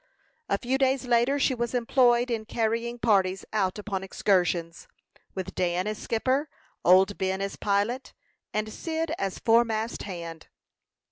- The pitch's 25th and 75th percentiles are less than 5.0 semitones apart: Yes, average, 4.1 semitones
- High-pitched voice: Yes, high, 220 Hz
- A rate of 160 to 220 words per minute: No, average, 140 wpm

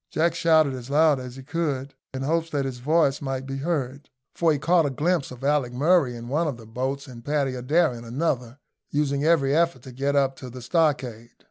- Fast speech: Yes, fast, 220 wpm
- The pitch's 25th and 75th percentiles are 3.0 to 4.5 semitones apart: Yes, average, 3.5 semitones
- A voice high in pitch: No, medium, 140 Hz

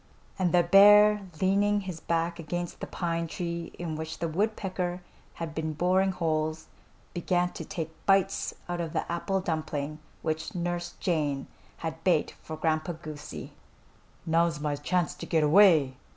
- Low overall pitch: No, medium, 170 Hz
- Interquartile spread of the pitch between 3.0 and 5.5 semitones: No, narrow, 2.4 semitones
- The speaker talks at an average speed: Yes, average, 150 wpm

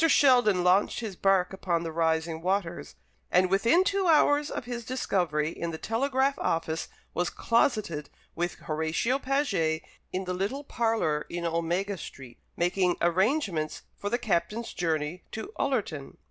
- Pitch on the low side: No, medium, 185 Hz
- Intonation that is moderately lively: No, wide, 6.1 semitones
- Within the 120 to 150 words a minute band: Yes, average, 145 wpm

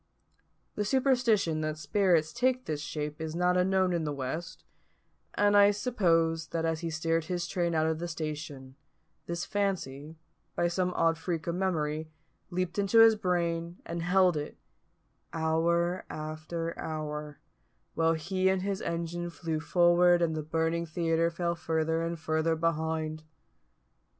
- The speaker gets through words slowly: No, average, 150 wpm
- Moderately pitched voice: Yes, medium, 165 Hz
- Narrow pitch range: Yes, narrow, 2.2 semitones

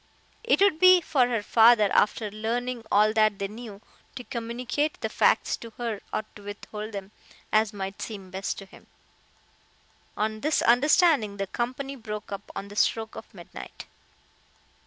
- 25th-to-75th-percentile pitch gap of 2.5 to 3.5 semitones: Yes, average, 3.1 semitones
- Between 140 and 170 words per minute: Yes, average, 160 wpm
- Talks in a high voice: Yes, high, 220 Hz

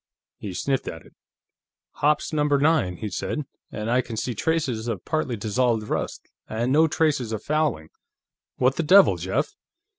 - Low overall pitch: Yes, low, 130 Hz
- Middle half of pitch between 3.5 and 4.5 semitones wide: No, wide, 5.6 semitones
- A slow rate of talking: No, average, 160 wpm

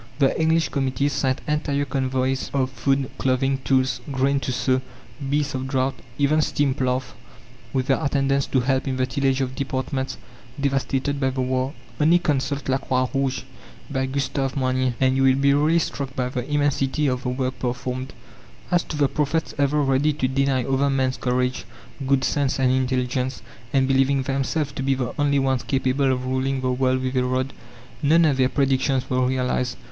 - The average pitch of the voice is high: No, low, 135 Hz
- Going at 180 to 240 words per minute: Yes, average, 185 wpm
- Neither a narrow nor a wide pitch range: No, narrow, 1.3 semitones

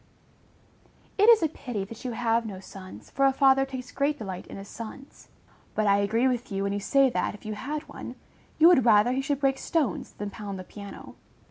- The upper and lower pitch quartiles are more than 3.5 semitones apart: Yes, average, 5.1 semitones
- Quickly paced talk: Yes, fast, 225 wpm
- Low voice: No, high, 235 Hz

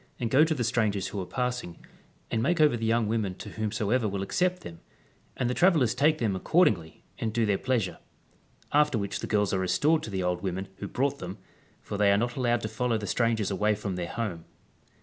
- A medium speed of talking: No, fast, 220 wpm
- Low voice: Yes, low, 110 Hz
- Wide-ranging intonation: No, average, 4.1 semitones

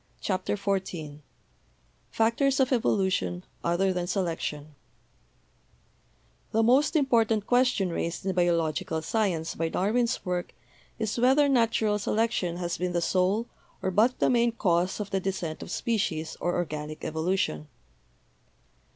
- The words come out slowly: Yes, slow, 130 wpm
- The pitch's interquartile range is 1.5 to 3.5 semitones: No, average, 4.8 semitones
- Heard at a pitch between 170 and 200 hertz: Yes, high, 190 Hz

